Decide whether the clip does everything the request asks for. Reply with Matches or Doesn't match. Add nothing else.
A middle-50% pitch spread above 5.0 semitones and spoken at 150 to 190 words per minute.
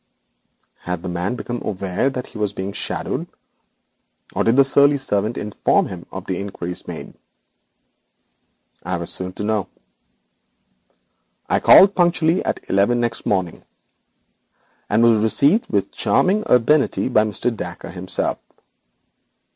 Doesn't match